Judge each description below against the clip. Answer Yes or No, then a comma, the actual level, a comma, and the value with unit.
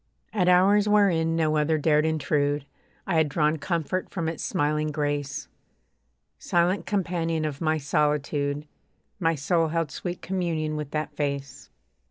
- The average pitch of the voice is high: No, medium, 155 Hz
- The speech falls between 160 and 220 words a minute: No, average, 140 wpm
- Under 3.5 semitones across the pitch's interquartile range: Yes, narrow, 2.4 semitones